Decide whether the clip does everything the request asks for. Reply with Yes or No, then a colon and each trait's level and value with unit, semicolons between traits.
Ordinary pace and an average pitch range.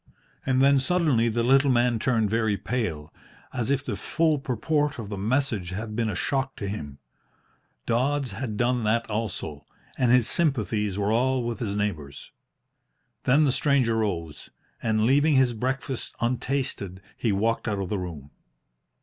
Yes: average, 160 wpm; average, 4.3 semitones